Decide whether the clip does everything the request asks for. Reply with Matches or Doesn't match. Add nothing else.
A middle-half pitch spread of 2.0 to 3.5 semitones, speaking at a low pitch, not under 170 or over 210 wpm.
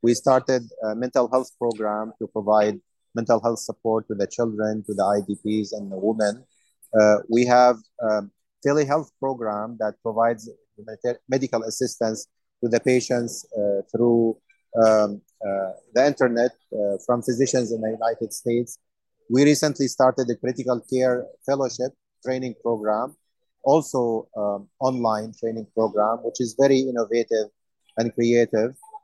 Doesn't match